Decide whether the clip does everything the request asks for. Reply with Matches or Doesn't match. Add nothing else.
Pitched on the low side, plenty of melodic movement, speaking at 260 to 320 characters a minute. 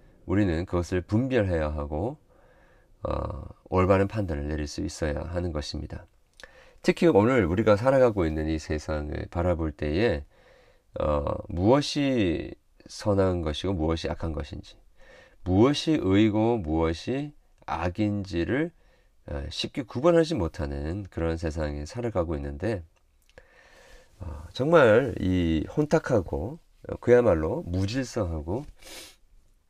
Doesn't match